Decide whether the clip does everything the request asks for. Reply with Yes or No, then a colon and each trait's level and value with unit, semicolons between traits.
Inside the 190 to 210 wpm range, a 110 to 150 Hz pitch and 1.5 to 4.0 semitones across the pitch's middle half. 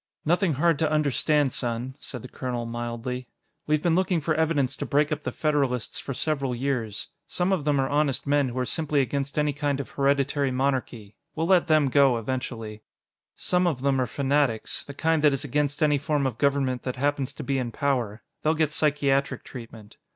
Yes: average, 195 wpm; medium, 140 Hz; average, 2.9 semitones